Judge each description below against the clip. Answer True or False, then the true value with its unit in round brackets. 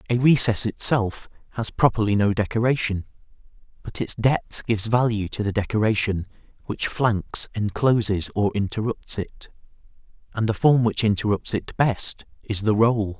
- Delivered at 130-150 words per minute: True (140 wpm)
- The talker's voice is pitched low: True (110 Hz)